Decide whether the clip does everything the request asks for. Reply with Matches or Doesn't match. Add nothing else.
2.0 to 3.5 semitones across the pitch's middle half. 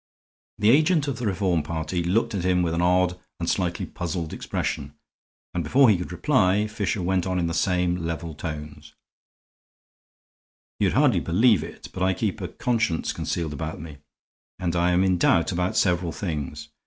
Matches